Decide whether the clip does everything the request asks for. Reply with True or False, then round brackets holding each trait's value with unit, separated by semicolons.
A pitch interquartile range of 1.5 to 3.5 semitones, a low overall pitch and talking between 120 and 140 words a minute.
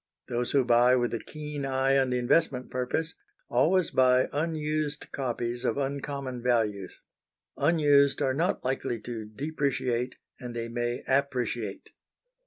True (3.0 semitones; 130 Hz; 135 wpm)